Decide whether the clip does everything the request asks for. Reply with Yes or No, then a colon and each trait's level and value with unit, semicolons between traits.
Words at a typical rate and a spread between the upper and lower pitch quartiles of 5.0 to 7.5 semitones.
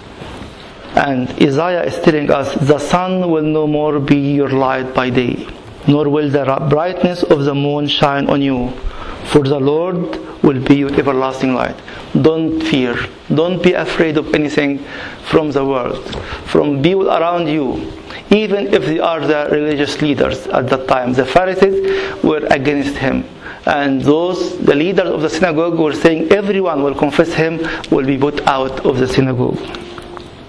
No: average, 160 wpm; average, 3.1 semitones